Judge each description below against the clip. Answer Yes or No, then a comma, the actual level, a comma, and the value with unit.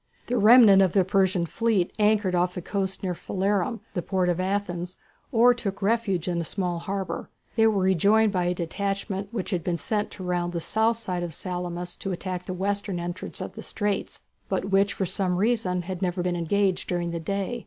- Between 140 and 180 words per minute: No, fast, 205 wpm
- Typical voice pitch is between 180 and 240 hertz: Yes, high, 190 Hz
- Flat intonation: Yes, narrow, 2.3 semitones